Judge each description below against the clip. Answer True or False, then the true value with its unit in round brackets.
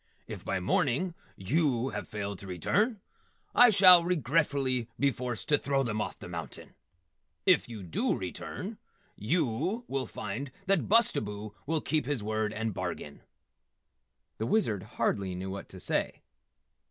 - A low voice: True (125 Hz)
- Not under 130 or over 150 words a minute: True (145 wpm)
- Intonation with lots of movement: True (7.4 semitones)